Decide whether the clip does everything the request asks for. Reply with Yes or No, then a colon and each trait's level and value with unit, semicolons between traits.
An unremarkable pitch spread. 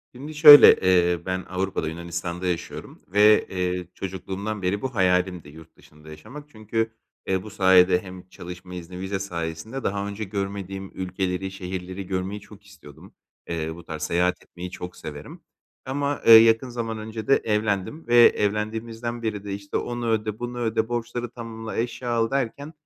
Yes: average, 3.7 semitones